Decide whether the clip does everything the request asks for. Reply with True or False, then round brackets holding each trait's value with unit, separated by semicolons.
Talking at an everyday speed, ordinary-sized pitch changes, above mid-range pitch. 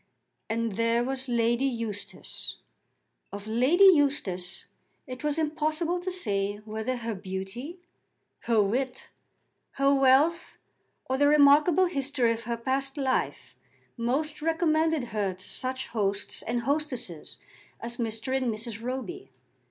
False (125 wpm; 4.4 semitones; 255 Hz)